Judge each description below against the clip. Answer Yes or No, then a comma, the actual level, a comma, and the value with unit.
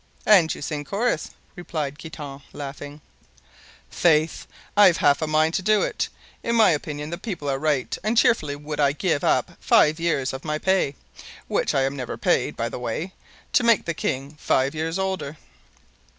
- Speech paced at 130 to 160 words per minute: No, average, 170 wpm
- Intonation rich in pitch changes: No, average, 4.0 semitones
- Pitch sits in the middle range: Yes, medium, 155 Hz